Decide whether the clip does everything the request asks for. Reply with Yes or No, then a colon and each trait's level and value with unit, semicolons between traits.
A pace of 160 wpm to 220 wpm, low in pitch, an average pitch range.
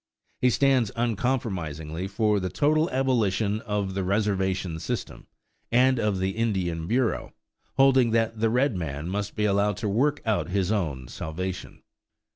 No: average, 145 wpm; low, 105 Hz; average, 4.1 semitones